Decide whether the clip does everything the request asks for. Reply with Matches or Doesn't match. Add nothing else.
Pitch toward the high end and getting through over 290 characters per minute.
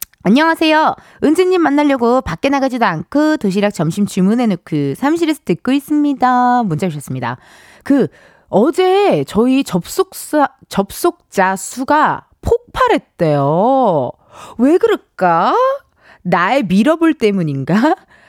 Doesn't match